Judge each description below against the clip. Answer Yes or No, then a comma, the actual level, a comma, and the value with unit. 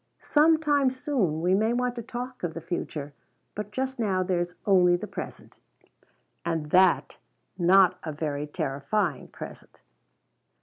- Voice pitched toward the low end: No, medium, 185 Hz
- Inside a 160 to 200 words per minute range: No, slow, 135 wpm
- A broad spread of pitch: Yes, wide, 6.8 semitones